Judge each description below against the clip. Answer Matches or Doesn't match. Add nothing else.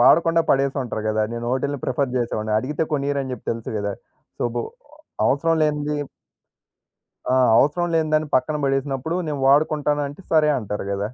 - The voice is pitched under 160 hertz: Matches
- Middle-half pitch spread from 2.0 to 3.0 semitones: Doesn't match